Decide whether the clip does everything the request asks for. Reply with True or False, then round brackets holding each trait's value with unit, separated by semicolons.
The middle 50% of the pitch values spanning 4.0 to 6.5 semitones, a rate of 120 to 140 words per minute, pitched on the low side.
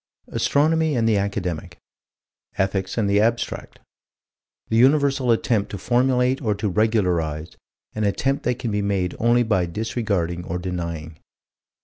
True (4.9 semitones; 135 wpm; 105 Hz)